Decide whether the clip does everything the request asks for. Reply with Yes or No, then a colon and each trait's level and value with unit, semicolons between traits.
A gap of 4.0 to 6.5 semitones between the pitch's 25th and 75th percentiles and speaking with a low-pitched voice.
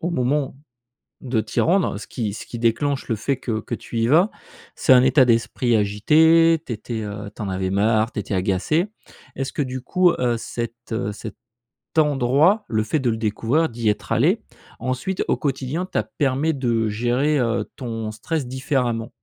Yes: average, 4.6 semitones; low, 120 Hz